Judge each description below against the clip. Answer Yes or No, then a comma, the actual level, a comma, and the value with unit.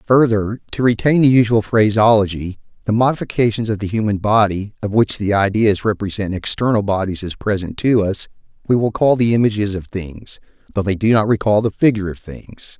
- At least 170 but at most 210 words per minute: Yes, average, 185 wpm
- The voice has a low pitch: Yes, low, 105 Hz